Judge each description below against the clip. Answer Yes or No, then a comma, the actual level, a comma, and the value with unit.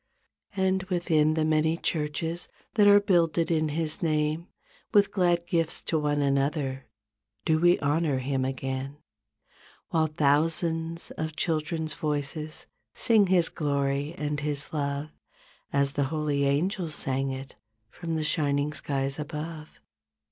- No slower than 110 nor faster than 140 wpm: Yes, slow, 135 wpm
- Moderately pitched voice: Yes, medium, 155 Hz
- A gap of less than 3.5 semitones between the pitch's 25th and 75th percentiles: Yes, average, 2.7 semitones